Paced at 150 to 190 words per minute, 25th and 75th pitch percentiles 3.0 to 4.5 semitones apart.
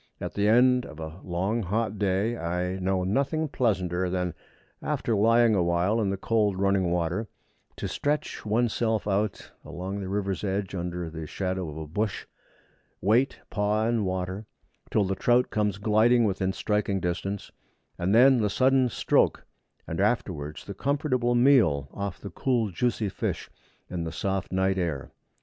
Yes: average, 165 wpm; average, 3.8 semitones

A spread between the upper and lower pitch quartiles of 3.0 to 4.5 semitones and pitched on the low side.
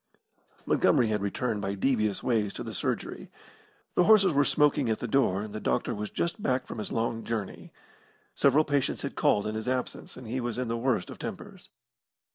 Yes: average, 4.0 semitones; low, 115 Hz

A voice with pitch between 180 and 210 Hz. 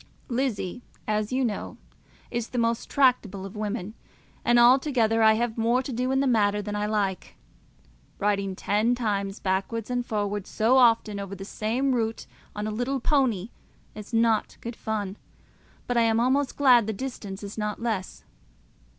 No: high, 225 Hz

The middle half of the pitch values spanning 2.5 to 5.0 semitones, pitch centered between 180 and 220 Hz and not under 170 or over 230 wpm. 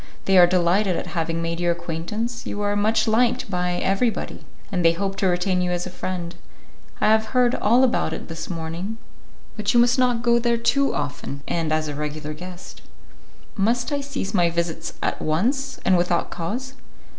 No: wide, 5.6 semitones; high, 190 Hz; average, 190 wpm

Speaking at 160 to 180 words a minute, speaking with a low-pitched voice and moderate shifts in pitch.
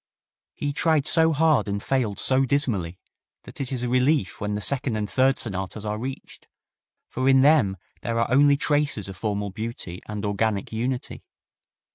Yes: average, 170 wpm; low, 120 Hz; average, 5.0 semitones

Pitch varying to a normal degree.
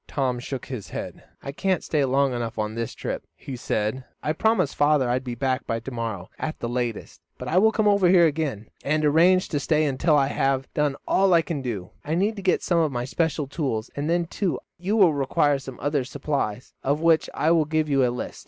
Yes: average, 4.4 semitones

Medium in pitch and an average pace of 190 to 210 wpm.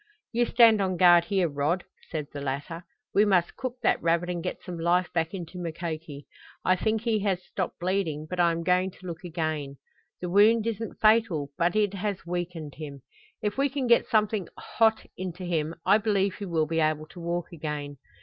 Yes: medium, 175 Hz; average, 200 wpm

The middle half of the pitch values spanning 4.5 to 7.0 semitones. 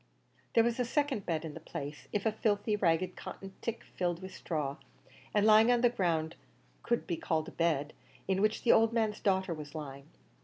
Yes: wide, 5.5 semitones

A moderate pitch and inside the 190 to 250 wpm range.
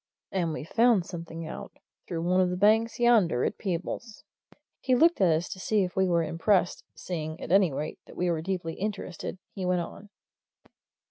Yes: medium, 180 Hz; average, 200 wpm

